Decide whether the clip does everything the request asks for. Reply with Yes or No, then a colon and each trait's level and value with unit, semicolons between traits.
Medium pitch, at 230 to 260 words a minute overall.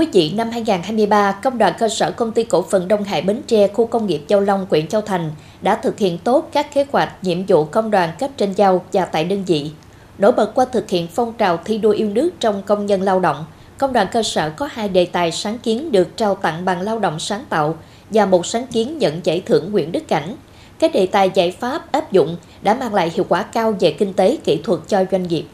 No: high, 205 Hz; fast, 250 wpm